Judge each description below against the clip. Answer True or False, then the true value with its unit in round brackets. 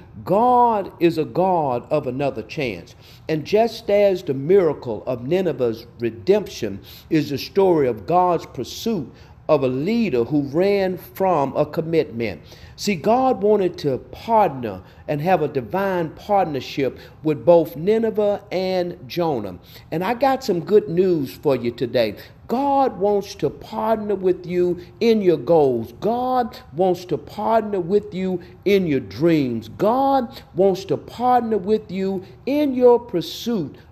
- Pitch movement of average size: False (6.9 semitones)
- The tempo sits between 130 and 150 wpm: True (140 wpm)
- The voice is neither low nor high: True (180 Hz)